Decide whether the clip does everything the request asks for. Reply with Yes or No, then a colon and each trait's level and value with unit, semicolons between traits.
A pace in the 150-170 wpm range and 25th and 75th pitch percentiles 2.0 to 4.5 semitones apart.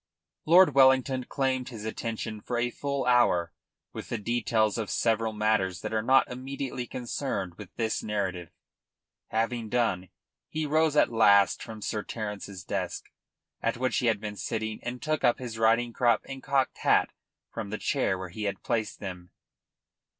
Yes: average, 165 wpm; average, 3.3 semitones